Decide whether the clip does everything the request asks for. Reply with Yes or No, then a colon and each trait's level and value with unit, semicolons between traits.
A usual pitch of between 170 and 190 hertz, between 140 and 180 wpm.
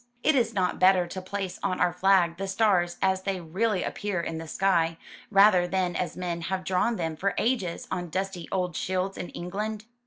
No: medium, 185 Hz; average, 195 wpm